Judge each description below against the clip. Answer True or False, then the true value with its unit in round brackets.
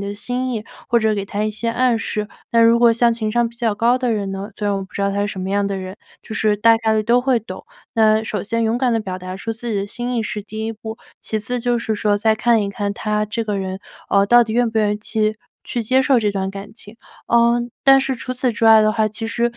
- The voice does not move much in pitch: True (2.3 semitones)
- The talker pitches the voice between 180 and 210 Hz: False (220 Hz)